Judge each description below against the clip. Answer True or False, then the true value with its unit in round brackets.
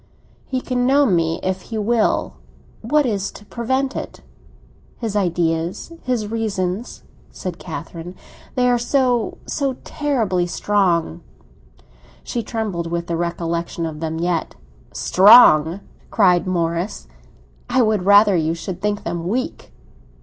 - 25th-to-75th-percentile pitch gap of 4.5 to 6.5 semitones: True (5.6 semitones)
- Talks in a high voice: True (195 Hz)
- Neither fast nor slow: False (125 wpm)